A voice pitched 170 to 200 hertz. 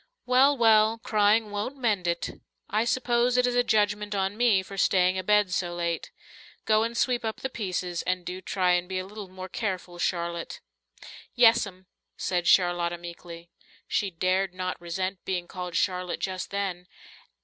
Yes: high, 190 Hz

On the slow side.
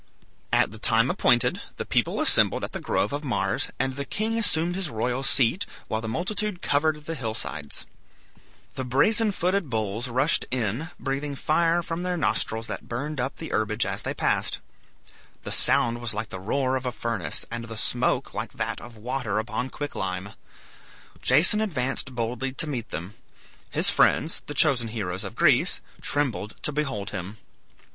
No: average, 175 wpm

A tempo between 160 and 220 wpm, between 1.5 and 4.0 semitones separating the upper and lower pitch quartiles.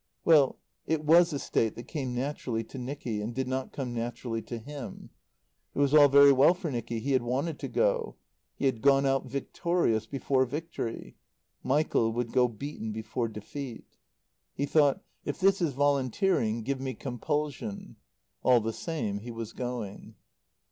Yes: average, 165 wpm; average, 3.7 semitones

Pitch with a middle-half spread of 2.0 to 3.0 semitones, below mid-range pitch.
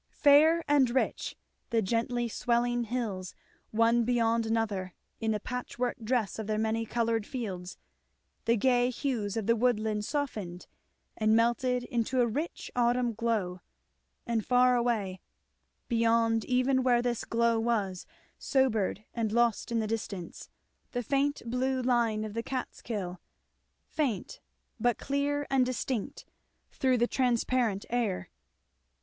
No: narrow, 2.4 semitones; high, 235 Hz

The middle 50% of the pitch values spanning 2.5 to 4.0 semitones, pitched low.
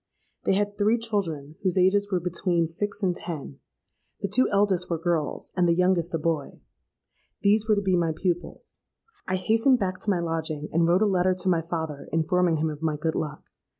No: average, 3.4 semitones; medium, 180 Hz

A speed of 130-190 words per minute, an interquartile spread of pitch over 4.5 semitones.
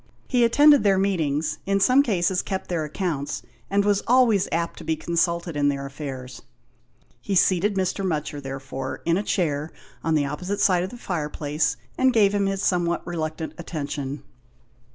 Yes: average, 170 wpm; average, 4.9 semitones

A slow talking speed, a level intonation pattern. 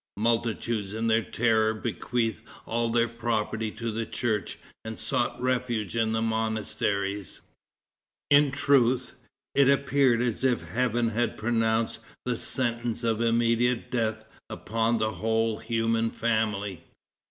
Yes: slow, 125 wpm; narrow, 1.4 semitones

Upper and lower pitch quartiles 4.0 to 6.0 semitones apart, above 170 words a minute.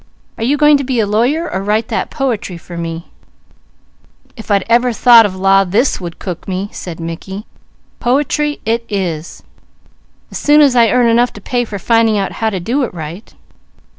Yes: average, 4.5 semitones; average, 195 wpm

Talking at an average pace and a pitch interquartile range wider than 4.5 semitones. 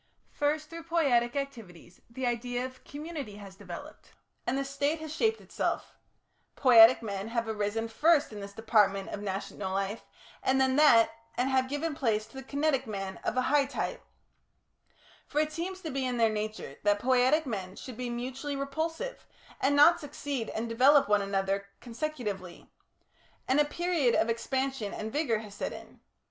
Yes: average, 170 wpm; average, 5.2 semitones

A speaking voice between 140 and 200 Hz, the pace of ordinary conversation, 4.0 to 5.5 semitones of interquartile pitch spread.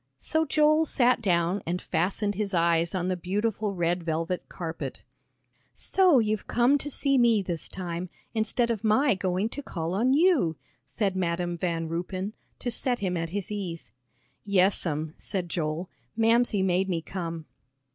Yes: high, 190 Hz; average, 155 wpm; average, 4.9 semitones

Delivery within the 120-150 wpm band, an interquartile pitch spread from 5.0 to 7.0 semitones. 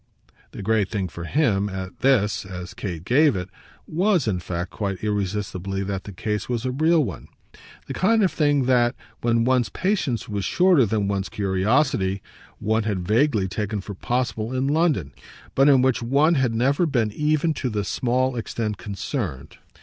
No: average, 175 wpm; wide, 5.6 semitones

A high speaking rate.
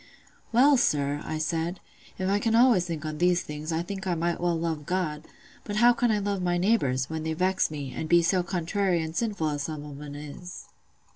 Yes: fast, 220 wpm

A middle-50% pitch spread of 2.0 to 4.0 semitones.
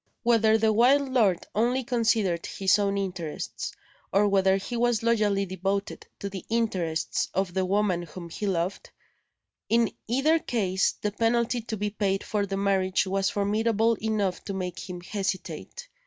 Yes: average, 3.1 semitones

